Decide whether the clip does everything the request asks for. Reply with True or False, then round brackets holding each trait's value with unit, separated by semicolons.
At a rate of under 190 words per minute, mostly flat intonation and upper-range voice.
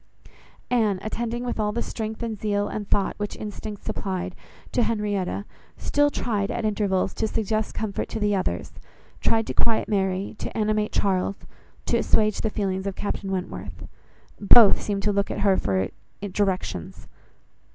True (160 wpm; 2.0 semitones; 205 Hz)